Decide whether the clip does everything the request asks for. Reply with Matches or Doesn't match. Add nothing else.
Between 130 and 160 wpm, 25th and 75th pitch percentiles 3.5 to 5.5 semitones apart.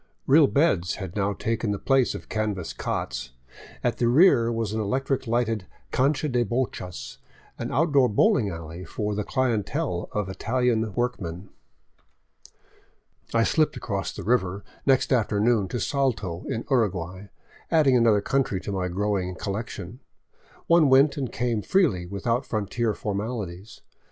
Matches